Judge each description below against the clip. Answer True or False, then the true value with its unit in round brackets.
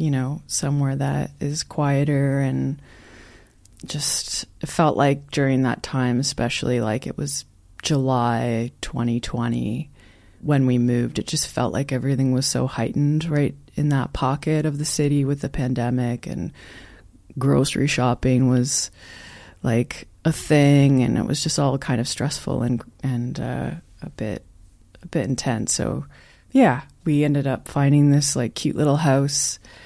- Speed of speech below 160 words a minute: True (150 wpm)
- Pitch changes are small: False (3.2 semitones)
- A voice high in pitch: False (135 Hz)